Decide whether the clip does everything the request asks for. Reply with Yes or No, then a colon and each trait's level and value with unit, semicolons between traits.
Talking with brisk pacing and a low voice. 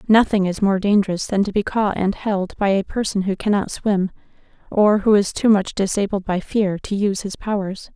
No: fast, 210 wpm; high, 200 Hz